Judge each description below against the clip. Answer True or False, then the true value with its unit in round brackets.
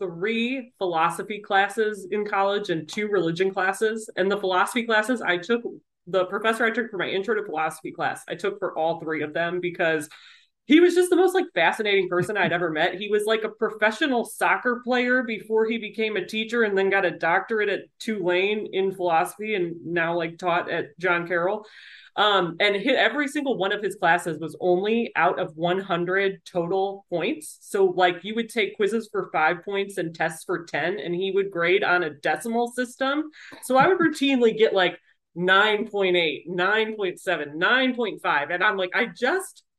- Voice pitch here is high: True (195 Hz)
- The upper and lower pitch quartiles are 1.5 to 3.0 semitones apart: False (4.0 semitones)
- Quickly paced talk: False (185 wpm)